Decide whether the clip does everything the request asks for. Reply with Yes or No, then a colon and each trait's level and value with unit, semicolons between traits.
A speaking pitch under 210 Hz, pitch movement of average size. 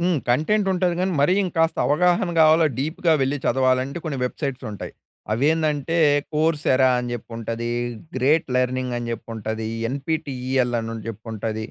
Yes: low, 135 Hz; average, 4.9 semitones